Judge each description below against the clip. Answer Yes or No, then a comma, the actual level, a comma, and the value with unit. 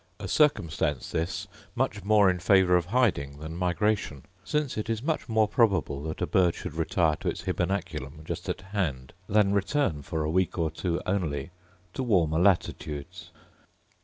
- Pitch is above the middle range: No, very low, 90 Hz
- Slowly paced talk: No, average, 165 wpm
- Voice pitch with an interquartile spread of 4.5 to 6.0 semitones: Yes, average, 4.8 semitones